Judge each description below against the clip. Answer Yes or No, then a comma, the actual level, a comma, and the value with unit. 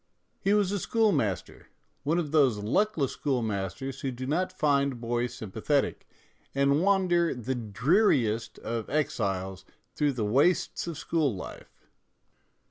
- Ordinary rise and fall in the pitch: No, wide, 6.5 semitones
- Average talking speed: No, slow, 130 wpm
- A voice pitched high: No, low, 135 Hz